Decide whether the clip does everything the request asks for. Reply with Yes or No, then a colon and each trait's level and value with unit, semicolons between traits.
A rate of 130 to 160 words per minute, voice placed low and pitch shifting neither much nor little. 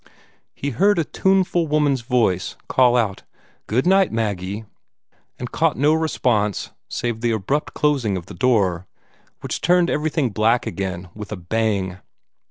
No: average, 145 wpm; low, 120 Hz; wide, 6.6 semitones